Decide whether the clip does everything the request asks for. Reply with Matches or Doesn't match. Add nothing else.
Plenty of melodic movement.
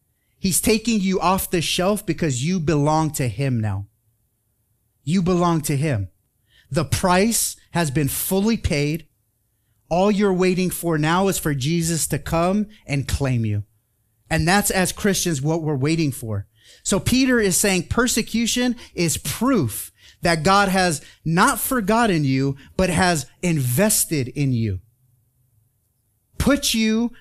Matches